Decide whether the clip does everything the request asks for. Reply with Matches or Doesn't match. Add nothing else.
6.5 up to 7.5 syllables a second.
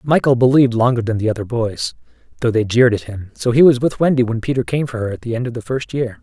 Matches